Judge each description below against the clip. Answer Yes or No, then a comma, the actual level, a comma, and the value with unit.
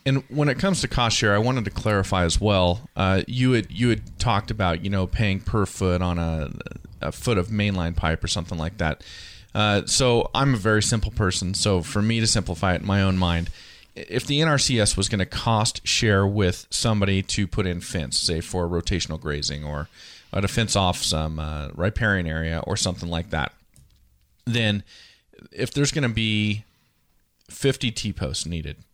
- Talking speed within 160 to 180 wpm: No, average, 195 wpm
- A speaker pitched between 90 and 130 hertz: Yes, low, 100 Hz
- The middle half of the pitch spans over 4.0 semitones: Yes, average, 4.4 semitones